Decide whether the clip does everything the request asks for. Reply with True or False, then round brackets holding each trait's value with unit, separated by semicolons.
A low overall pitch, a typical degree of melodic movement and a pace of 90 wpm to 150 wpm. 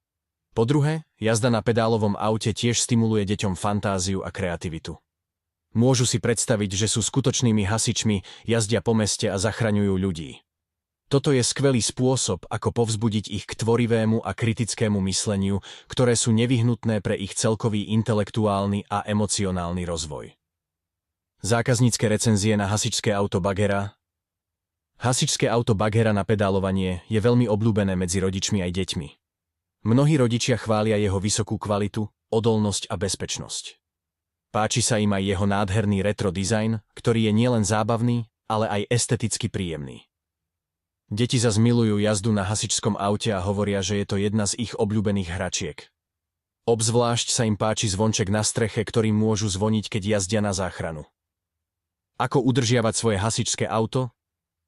True (105 Hz; 3.1 semitones; 135 wpm)